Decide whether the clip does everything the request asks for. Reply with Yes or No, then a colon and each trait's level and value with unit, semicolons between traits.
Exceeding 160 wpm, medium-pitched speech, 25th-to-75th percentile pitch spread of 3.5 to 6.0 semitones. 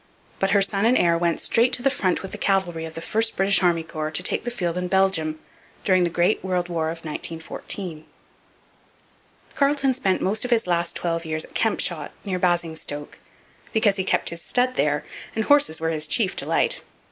Yes: average, 195 wpm; medium, 180 Hz; average, 4.1 semitones